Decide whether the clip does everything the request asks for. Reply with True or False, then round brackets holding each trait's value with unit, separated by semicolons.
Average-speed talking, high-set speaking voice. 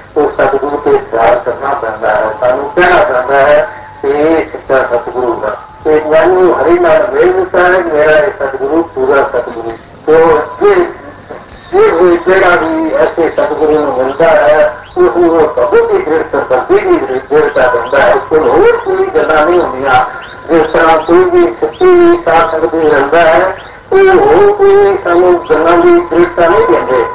True (140 wpm; 200 Hz)